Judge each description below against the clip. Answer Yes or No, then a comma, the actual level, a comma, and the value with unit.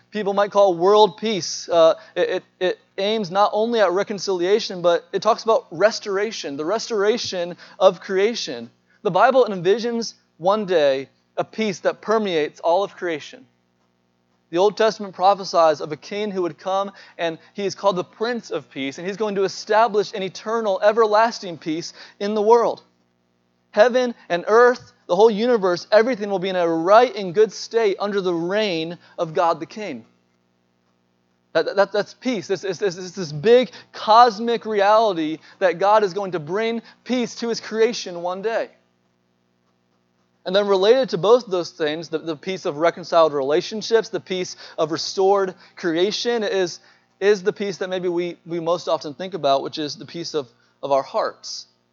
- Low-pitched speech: No, high, 190 Hz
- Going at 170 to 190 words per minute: Yes, average, 175 wpm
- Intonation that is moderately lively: Yes, average, 4.7 semitones